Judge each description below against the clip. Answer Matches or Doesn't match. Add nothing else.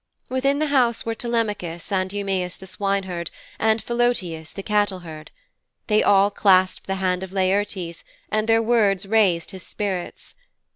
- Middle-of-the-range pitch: Doesn't match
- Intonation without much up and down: Doesn't match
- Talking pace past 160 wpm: Doesn't match